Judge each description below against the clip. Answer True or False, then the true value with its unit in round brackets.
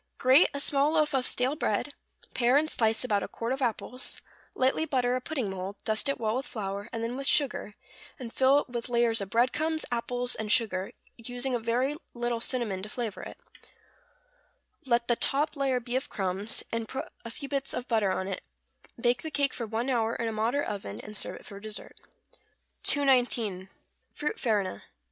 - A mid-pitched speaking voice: False (240 Hz)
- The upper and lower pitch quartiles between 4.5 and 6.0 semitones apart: False (3.5 semitones)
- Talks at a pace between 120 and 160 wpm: False (200 wpm)